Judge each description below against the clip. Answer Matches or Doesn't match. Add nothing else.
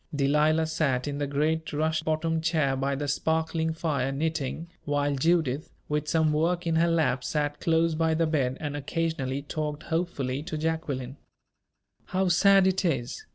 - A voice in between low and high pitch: Matches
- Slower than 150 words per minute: Doesn't match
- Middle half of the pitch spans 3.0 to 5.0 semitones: Doesn't match